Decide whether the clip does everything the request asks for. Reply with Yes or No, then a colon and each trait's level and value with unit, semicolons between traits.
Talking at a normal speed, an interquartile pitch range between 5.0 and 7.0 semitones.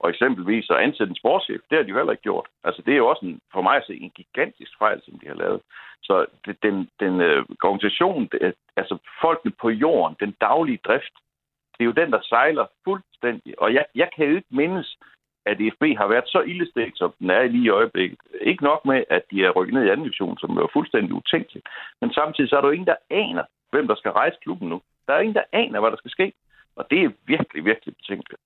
No: fast, 240 wpm; wide, 5.6 semitones